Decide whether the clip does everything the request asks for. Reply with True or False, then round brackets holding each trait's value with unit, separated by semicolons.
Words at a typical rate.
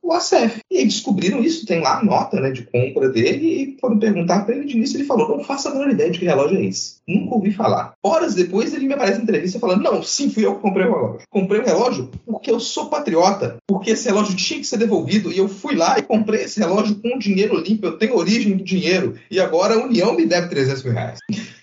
False (255 wpm)